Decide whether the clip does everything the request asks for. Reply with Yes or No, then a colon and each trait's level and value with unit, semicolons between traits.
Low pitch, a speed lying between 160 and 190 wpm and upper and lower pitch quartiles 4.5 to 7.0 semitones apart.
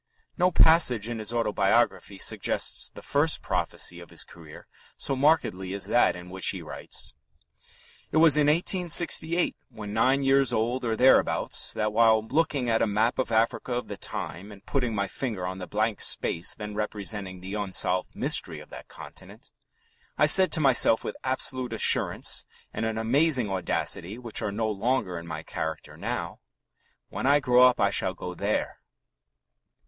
Yes: low, 110 Hz; average, 170 wpm; average, 4.9 semitones